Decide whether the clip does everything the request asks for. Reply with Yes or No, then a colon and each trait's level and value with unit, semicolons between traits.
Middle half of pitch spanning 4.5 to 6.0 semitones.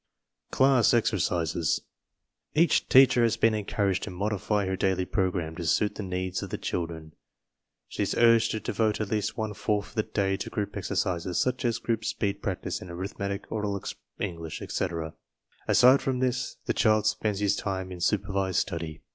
No: average, 3.0 semitones